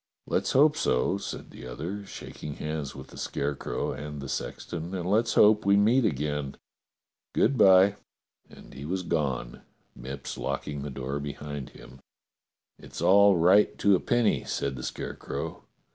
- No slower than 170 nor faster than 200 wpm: No, average, 160 wpm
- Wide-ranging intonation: Yes, wide, 6.3 semitones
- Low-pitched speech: Yes, very low, 75 Hz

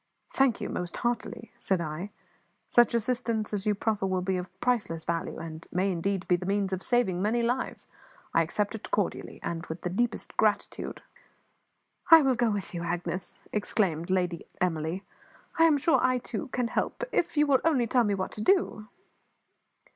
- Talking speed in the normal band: Yes, average, 180 wpm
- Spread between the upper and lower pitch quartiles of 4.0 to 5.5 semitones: Yes, average, 5.2 semitones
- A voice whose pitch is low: No, high, 205 Hz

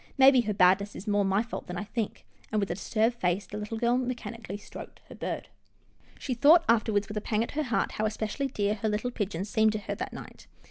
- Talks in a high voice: Yes, high, 215 Hz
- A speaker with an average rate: No, fast, 235 wpm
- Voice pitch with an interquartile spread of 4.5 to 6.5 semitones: No, average, 2.7 semitones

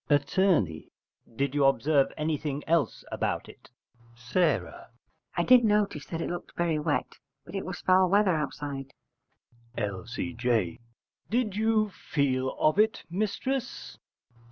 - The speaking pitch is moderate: Yes, medium, 155 Hz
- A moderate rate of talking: No, slow, 125 wpm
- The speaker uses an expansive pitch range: Yes, wide, 6.2 semitones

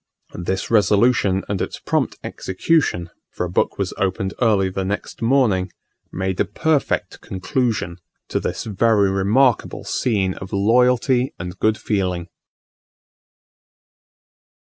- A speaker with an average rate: No, slow, 120 wpm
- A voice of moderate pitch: No, low, 100 Hz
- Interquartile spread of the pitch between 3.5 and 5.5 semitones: Yes, average, 3.8 semitones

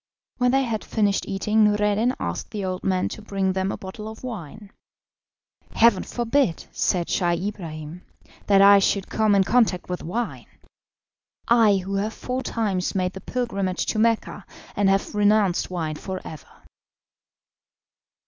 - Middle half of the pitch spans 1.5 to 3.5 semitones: Yes, average, 2.8 semitones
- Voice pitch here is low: No, high, 200 Hz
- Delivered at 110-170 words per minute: Yes, average, 150 wpm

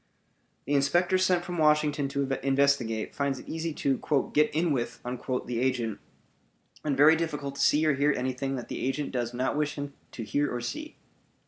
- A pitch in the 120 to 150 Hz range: Yes, medium, 140 Hz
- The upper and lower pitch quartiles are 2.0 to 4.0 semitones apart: Yes, average, 3.0 semitones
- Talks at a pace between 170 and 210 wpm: Yes, average, 185 wpm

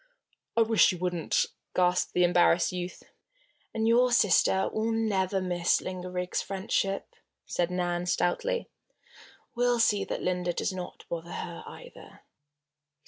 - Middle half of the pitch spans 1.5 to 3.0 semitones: No, average, 3.5 semitones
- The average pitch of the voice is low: No, medium, 185 Hz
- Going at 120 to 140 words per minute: Yes, slow, 135 wpm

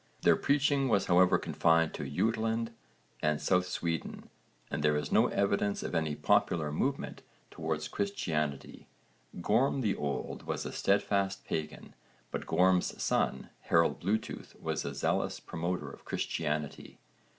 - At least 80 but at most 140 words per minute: Yes, slow, 135 wpm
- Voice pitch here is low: Yes, very low, 90 Hz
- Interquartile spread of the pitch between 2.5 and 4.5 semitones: No, average, 5.0 semitones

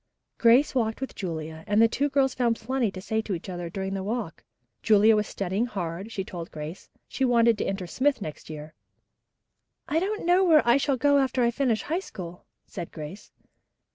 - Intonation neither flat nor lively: No, wide, 6.1 semitones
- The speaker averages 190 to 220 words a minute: Yes, average, 200 wpm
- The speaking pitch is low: No, high, 220 Hz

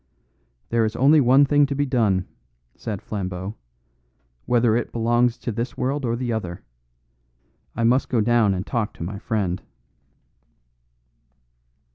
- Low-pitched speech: Yes, low, 115 Hz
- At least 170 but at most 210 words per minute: No, average, 140 wpm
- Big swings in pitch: No, average, 3.4 semitones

